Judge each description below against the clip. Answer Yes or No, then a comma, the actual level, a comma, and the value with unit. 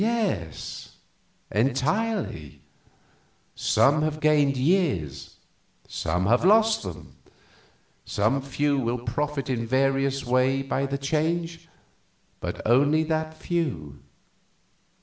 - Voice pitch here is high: No, medium, 140 Hz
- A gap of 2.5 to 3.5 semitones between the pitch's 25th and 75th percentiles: No, average, 4.7 semitones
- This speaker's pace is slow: Yes, slow, 95 wpm